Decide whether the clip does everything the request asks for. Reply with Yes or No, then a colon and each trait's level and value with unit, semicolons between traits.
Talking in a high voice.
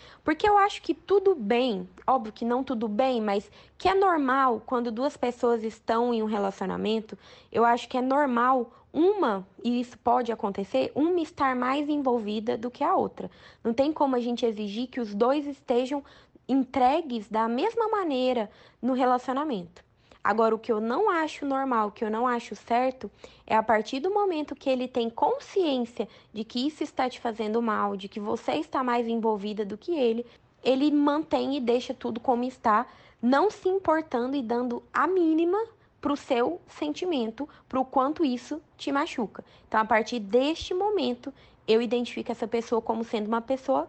Yes: very high, 250 Hz